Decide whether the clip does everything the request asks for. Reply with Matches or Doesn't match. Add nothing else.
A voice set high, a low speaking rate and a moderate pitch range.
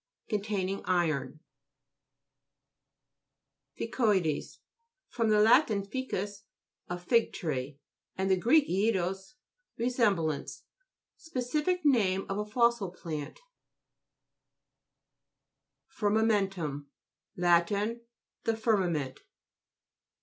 Matches